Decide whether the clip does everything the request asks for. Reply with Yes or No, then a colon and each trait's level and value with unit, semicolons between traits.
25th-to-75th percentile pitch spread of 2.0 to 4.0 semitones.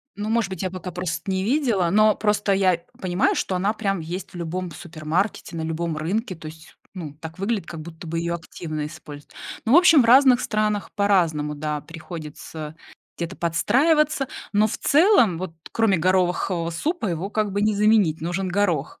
No: average, 4.4 semitones